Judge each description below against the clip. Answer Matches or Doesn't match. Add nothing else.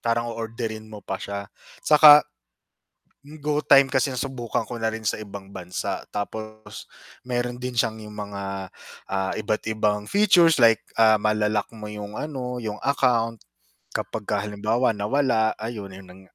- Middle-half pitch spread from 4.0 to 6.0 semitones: Doesn't match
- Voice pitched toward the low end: Matches